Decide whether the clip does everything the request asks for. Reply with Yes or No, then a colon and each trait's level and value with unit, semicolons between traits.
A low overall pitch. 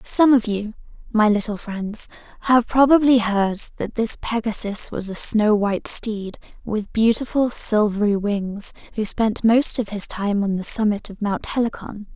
No: high, 215 Hz